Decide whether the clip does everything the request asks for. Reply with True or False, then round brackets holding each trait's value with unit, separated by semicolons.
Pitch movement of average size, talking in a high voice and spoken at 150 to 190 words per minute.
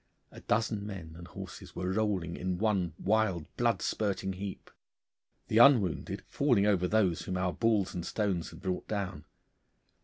False (3.0 semitones; 95 Hz; 155 wpm)